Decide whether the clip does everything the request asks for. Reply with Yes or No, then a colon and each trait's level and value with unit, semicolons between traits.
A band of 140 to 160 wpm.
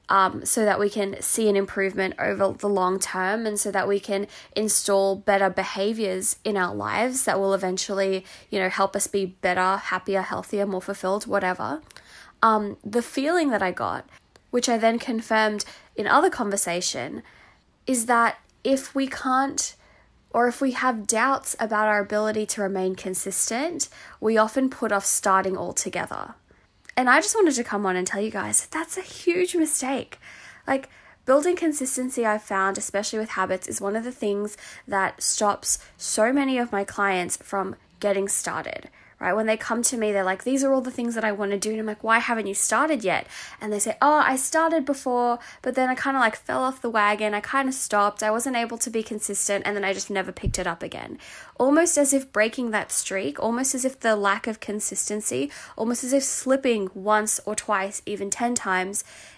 No: average, 195 wpm